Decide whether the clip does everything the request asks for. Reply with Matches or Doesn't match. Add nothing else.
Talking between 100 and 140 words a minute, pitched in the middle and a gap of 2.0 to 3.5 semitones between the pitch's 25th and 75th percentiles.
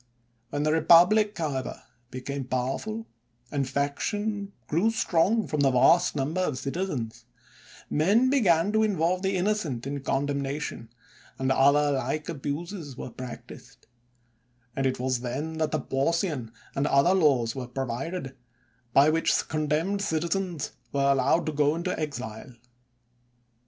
Doesn't match